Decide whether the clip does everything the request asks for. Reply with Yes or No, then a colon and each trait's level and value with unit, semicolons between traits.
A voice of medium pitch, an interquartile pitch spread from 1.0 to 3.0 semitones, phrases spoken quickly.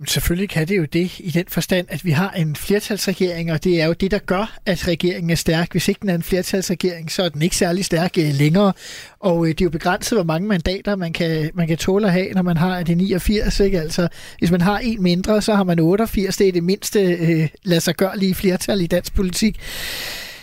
Yes: medium, 180 Hz; narrow, 2.4 semitones; fast, 235 wpm